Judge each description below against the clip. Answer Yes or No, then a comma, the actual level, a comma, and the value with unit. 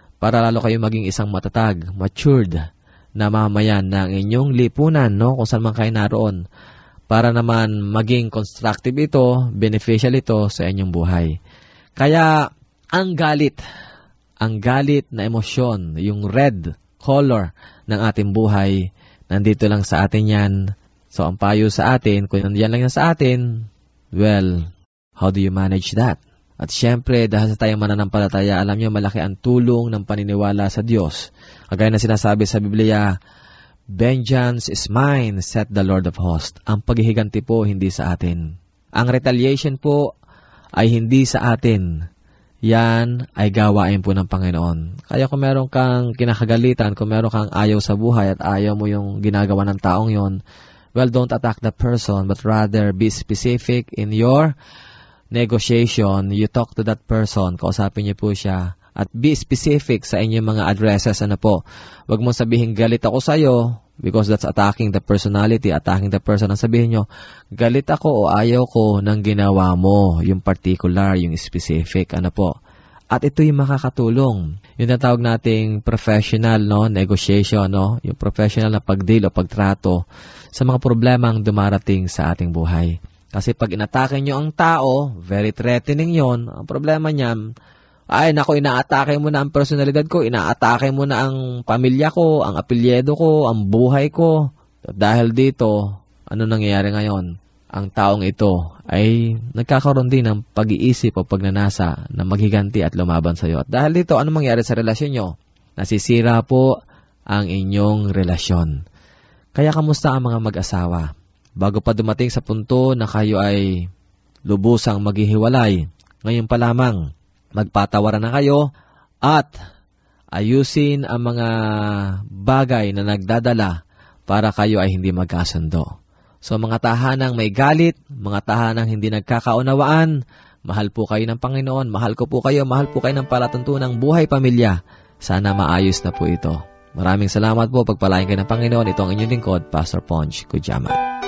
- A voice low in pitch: Yes, low, 110 Hz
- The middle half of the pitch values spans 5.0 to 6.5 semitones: No, average, 3.8 semitones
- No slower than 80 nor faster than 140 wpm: No, average, 150 wpm